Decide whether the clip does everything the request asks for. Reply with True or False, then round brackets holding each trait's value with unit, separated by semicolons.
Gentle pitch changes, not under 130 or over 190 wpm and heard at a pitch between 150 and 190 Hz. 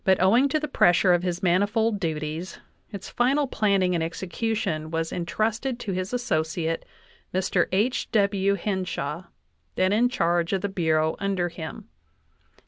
False (4.2 semitones; 145 wpm; 185 Hz)